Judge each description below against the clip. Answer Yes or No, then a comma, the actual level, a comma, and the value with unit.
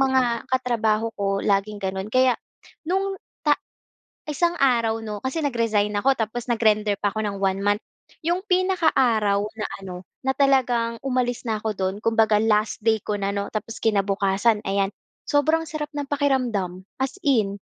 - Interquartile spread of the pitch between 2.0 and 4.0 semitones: No, average, 4.4 semitones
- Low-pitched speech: No, high, 225 Hz